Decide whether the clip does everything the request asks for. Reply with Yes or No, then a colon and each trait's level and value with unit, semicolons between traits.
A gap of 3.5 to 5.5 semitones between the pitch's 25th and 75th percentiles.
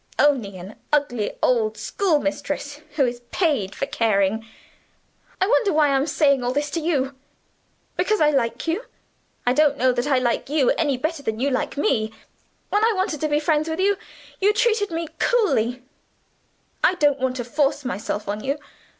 Yes: average, 4.5 semitones